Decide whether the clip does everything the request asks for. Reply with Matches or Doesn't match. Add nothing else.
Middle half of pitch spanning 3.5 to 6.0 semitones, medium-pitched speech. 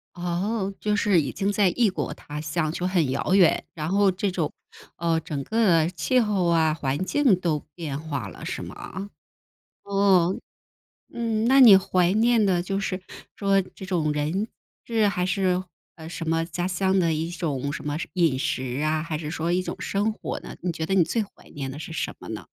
Matches